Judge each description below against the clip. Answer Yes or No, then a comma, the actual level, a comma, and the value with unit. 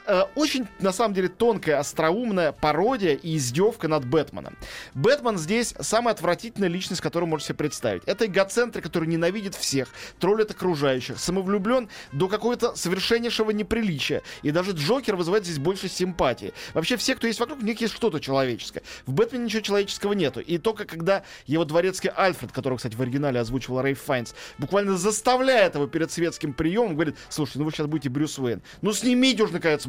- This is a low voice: No, medium, 185 Hz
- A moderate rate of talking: No, fast, 175 wpm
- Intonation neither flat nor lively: No, wide, 6.4 semitones